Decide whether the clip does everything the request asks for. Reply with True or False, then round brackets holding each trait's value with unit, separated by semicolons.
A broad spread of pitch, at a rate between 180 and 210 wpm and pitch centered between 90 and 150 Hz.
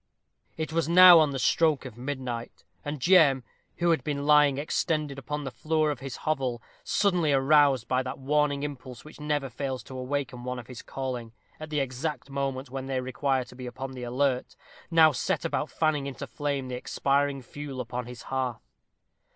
False (2.6 semitones; 185 wpm; 135 Hz)